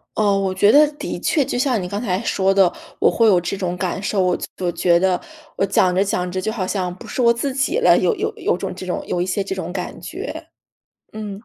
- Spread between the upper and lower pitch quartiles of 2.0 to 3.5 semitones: Yes, average, 3.0 semitones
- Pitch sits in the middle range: No, high, 195 Hz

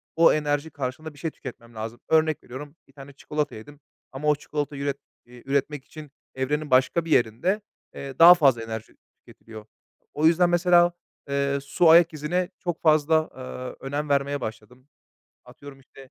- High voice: No, medium, 145 Hz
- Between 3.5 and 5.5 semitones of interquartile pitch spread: No, average, 3.1 semitones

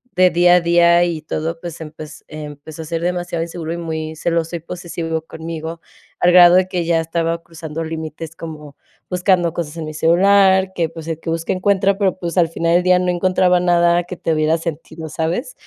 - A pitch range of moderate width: No, narrow, 1.7 semitones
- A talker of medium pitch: Yes, medium, 170 Hz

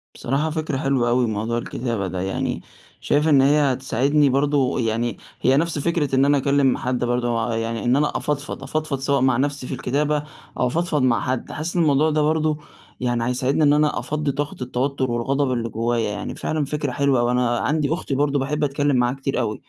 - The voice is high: No, low, 135 Hz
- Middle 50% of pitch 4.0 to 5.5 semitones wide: No, average, 3.2 semitones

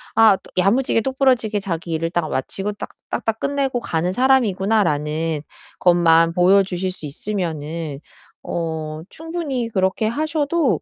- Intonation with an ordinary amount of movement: No, wide, 6.5 semitones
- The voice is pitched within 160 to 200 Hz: Yes, high, 190 Hz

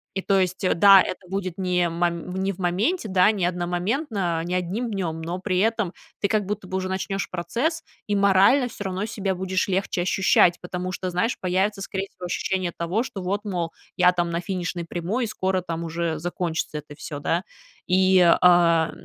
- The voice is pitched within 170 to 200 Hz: Yes, medium, 185 Hz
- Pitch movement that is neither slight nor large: No, narrow, 2.1 semitones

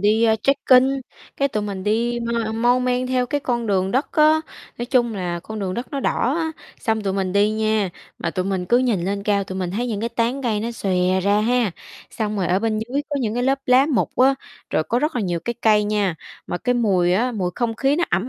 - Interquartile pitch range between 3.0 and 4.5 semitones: Yes, average, 3.9 semitones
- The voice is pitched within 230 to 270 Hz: No, high, 220 Hz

